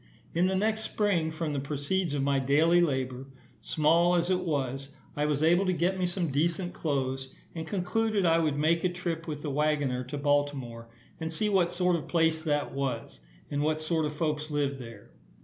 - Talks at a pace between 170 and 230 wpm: Yes, average, 200 wpm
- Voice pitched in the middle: Yes, medium, 155 Hz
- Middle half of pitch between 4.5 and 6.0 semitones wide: No, average, 3.6 semitones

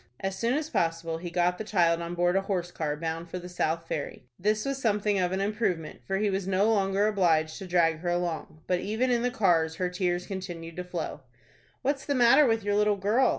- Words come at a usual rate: No, fast, 230 wpm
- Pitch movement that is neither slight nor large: Yes, average, 3.7 semitones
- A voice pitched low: No, medium, 185 Hz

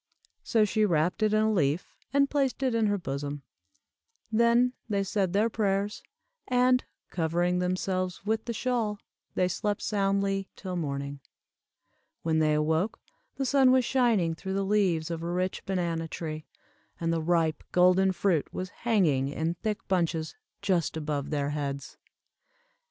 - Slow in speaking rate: No, average, 150 wpm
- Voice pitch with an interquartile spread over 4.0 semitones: Yes, average, 4.8 semitones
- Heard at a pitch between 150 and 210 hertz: Yes, medium, 185 Hz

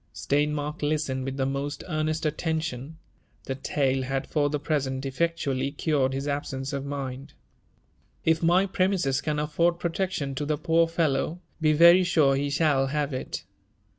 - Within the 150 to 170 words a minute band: Yes, average, 160 wpm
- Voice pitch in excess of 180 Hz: No, medium, 145 Hz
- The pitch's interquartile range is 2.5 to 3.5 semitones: Yes, average, 2.9 semitones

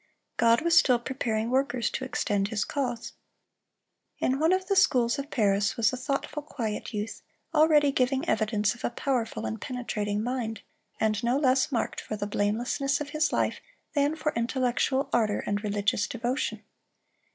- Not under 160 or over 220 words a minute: Yes, average, 165 wpm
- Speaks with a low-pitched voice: No, high, 245 Hz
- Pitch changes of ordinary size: Yes, average, 4.2 semitones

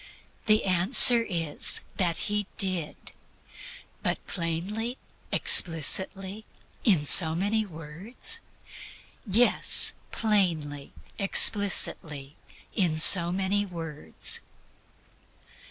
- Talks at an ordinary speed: No, slow, 75 wpm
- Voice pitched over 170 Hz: Yes, medium, 185 Hz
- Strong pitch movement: No, average, 4.2 semitones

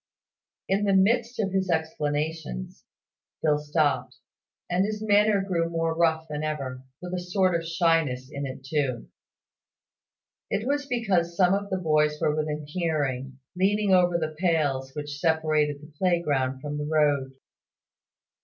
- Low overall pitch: No, medium, 160 Hz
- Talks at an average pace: Yes, average, 145 wpm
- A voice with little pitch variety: No, average, 3.9 semitones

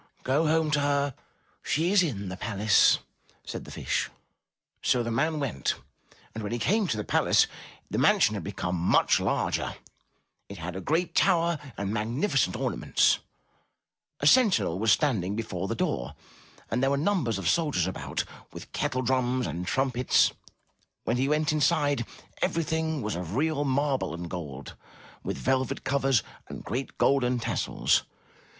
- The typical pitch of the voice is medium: No, low, 130 Hz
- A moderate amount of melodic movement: No, wide, 6.8 semitones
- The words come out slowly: No, average, 155 wpm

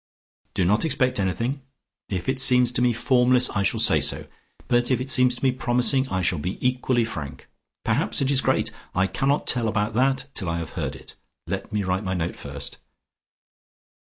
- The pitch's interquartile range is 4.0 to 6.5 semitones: Yes, wide, 5.4 semitones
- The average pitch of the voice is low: Yes, low, 120 Hz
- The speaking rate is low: No, average, 200 wpm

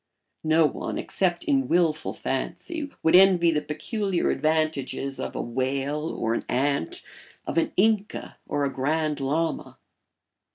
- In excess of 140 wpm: No, slow, 135 wpm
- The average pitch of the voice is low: No, medium, 155 Hz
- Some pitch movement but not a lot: Yes, average, 4.1 semitones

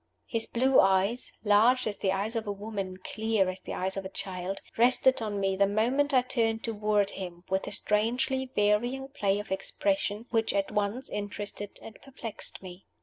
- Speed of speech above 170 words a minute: Yes, average, 185 wpm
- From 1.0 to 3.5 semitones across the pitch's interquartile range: Yes, average, 2.9 semitones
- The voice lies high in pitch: Yes, high, 210 Hz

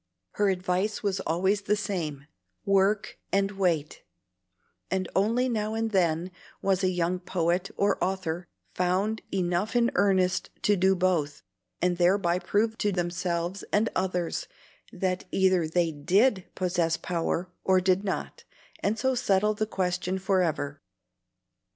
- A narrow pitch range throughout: Yes, narrow, 2.3 semitones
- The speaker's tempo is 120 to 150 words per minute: Yes, slow, 135 wpm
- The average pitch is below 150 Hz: No, medium, 185 Hz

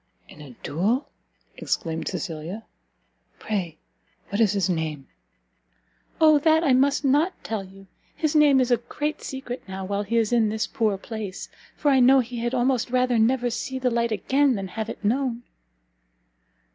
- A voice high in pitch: Yes, high, 235 Hz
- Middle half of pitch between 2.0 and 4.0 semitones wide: No, average, 4.8 semitones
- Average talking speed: Yes, average, 170 wpm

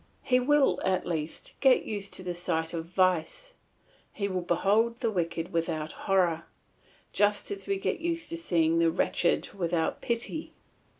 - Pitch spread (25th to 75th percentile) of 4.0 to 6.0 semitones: Yes, wide, 5.4 semitones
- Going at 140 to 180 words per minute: Yes, average, 160 wpm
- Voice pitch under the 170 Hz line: No, medium, 185 Hz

